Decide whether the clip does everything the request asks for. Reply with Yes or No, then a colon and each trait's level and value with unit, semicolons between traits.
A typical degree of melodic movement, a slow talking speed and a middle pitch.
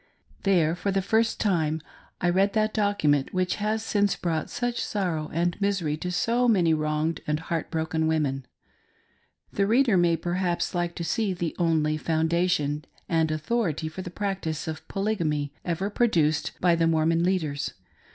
No: average, 3.8 semitones; average, 160 wpm; medium, 170 Hz